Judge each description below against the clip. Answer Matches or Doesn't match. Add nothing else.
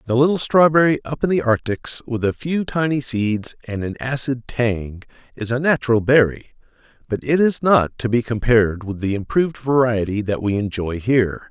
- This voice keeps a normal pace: Matches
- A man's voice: Matches